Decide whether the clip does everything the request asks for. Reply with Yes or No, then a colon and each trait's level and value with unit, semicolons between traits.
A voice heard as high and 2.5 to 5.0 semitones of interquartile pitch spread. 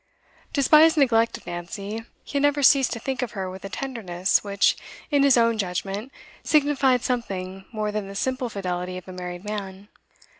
No: high, 215 Hz; wide, 5.6 semitones